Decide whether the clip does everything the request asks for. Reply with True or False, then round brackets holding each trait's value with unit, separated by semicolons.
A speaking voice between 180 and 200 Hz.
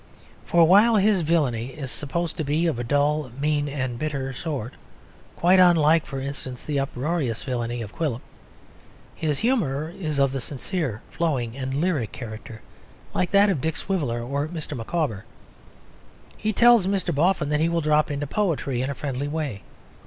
False (150 Hz)